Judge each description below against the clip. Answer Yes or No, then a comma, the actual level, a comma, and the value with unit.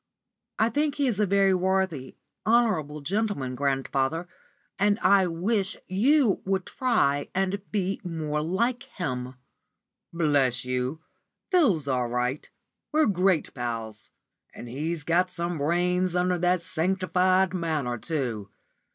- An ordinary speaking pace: No, slow, 125 wpm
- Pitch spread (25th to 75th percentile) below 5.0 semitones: No, wide, 5.5 semitones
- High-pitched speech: No, medium, 175 Hz